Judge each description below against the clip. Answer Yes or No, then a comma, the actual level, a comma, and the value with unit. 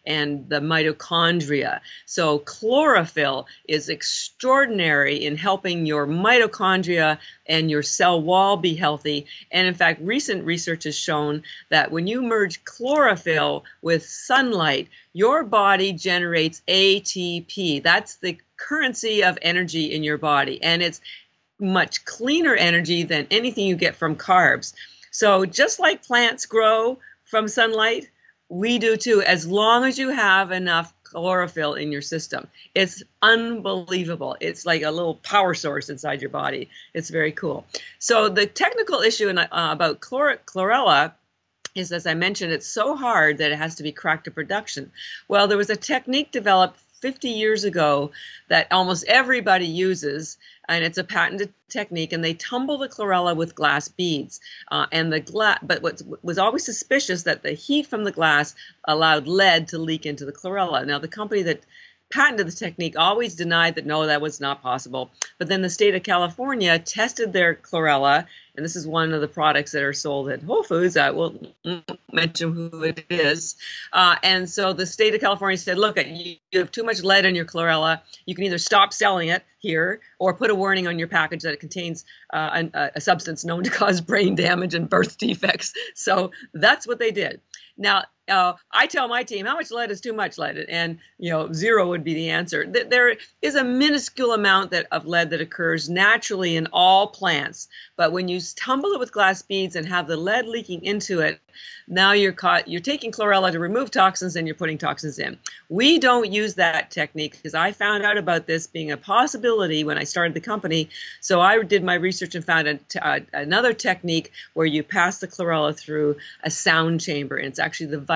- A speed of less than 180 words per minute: No, average, 185 wpm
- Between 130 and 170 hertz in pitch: No, medium, 180 Hz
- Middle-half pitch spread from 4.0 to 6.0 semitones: Yes, average, 4.4 semitones